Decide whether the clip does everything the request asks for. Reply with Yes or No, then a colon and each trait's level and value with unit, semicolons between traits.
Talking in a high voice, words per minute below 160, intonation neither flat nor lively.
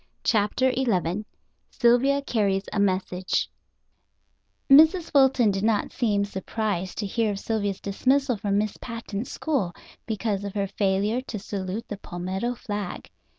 Yes: high, 210 Hz; slow, 135 wpm; average, 3.6 semitones